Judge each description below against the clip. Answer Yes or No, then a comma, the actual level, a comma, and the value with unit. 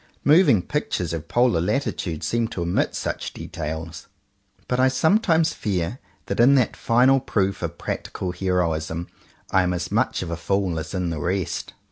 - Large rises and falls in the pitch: Yes, wide, 6.8 semitones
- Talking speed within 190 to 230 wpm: No, average, 165 wpm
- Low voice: Yes, very low, 95 Hz